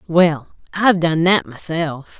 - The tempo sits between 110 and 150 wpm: Yes, slow, 135 wpm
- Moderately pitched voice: Yes, medium, 170 Hz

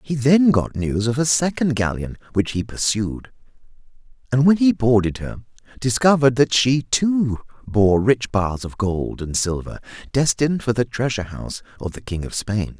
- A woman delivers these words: No, male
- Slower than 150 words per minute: No, average, 175 wpm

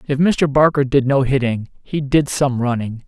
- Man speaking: Yes, male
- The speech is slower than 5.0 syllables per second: Yes, 4.6 syllables/s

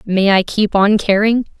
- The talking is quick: No, average, 190 wpm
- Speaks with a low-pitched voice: No, high, 205 Hz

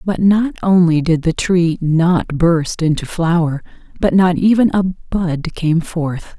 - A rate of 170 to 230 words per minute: No, average, 160 wpm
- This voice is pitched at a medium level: Yes, medium, 170 Hz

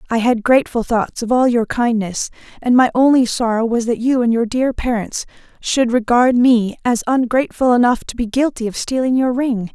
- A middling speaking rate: Yes, average, 195 wpm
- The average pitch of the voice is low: No, high, 240 Hz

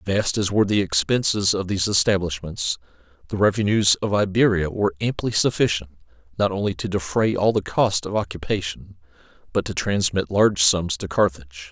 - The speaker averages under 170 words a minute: Yes, average, 160 wpm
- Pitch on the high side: No, very low, 95 Hz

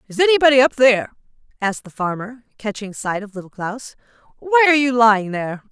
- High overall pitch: Yes, high, 230 Hz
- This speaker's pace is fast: No, average, 180 wpm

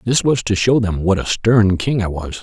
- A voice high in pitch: No, low, 105 Hz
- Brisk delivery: Yes, fast, 270 wpm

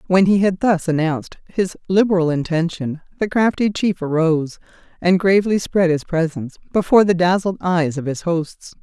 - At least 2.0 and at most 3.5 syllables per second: No, 5.1 syllables/s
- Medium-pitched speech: Yes, medium, 180 Hz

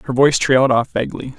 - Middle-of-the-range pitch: No, low, 130 Hz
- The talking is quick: Yes, fast, 215 wpm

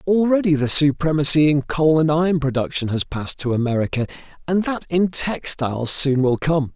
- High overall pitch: No, medium, 150 Hz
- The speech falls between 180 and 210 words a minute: No, average, 170 wpm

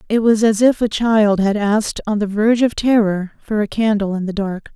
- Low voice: No, high, 210 Hz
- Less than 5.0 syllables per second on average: No, 5.3 syllables/s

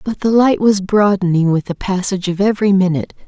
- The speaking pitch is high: Yes, high, 195 Hz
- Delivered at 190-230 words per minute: Yes, average, 200 wpm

